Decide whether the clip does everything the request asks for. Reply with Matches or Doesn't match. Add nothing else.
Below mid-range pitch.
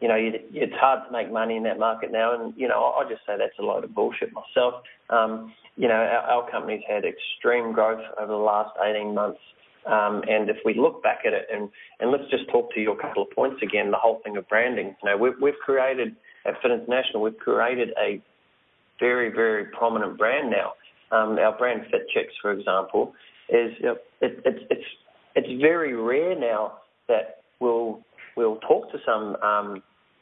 Matches